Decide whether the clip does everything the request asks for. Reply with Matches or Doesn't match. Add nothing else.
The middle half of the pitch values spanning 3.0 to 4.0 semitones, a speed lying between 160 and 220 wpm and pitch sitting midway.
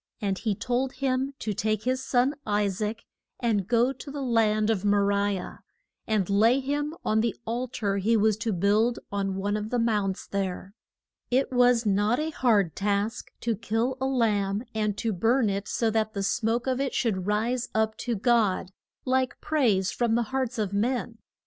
Doesn't match